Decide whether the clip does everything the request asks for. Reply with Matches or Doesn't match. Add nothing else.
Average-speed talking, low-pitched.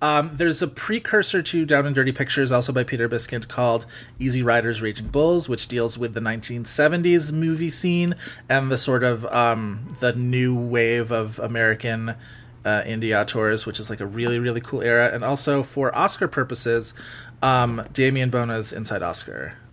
Matches